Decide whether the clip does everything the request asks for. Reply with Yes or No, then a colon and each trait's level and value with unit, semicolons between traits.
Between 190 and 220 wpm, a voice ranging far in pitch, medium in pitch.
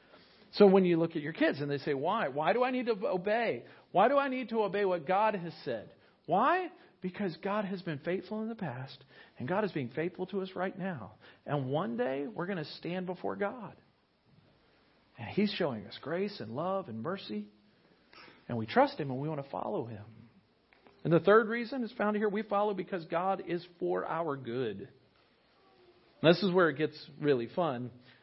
Yes: fast, 205 wpm; wide, 5.9 semitones; medium, 180 Hz